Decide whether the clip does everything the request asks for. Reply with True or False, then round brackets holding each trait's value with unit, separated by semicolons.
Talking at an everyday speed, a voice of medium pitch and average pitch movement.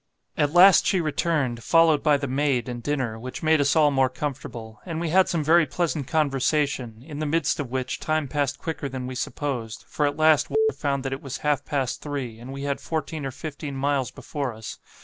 False (215 wpm; 145 Hz; 3.1 semitones)